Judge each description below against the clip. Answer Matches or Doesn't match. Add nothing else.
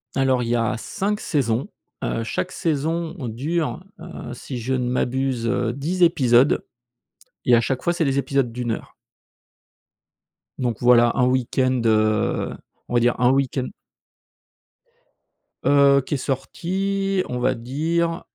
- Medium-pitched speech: Doesn't match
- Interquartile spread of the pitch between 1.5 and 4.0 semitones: Doesn't match